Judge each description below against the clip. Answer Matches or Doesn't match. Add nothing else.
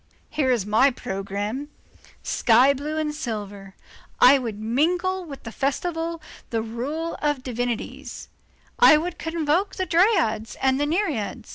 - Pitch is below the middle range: Doesn't match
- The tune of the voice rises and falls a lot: Matches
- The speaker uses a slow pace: Matches